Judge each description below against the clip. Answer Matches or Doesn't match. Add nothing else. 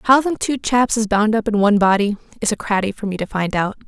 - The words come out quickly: Matches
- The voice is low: Doesn't match